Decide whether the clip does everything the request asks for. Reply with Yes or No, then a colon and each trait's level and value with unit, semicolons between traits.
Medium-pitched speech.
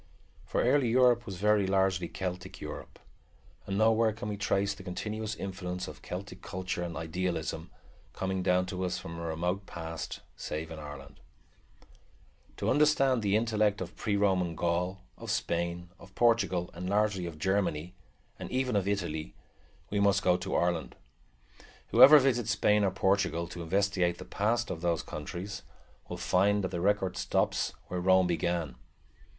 No: very low, 95 Hz